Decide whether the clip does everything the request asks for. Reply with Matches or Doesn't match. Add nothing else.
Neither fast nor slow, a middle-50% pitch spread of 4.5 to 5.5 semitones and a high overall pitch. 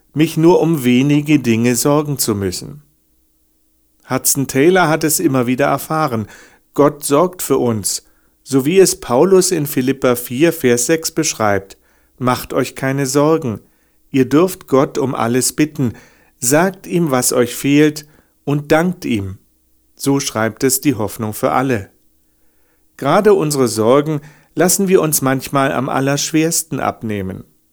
Doesn't match